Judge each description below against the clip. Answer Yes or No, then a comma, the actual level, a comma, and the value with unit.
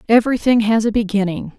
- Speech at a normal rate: Yes, average, 150 wpm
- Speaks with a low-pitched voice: No, high, 220 Hz